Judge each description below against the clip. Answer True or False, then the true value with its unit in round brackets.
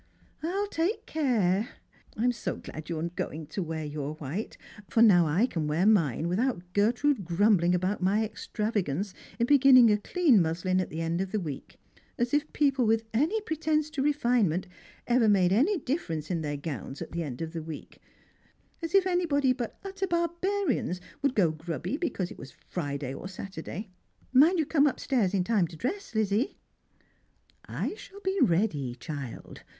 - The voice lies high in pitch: True (210 Hz)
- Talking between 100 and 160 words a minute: False (180 wpm)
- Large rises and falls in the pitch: True (8.9 semitones)